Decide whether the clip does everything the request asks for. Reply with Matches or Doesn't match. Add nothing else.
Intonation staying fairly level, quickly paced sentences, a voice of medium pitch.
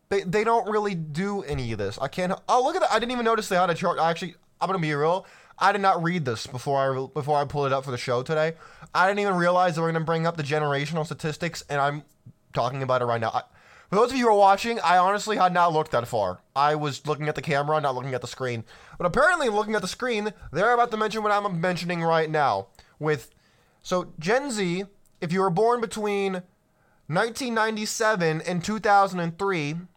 Doesn't match